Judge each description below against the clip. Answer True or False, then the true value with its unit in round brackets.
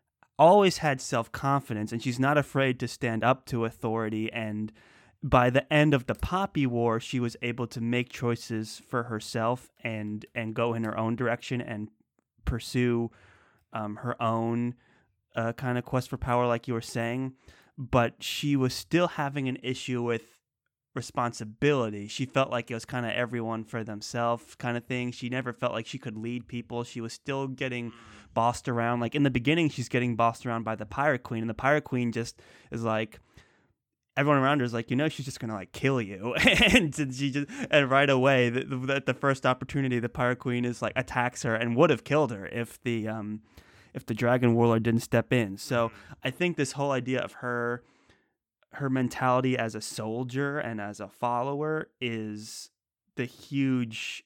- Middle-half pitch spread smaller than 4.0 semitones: True (2.5 semitones)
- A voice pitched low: True (120 Hz)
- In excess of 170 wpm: True (190 wpm)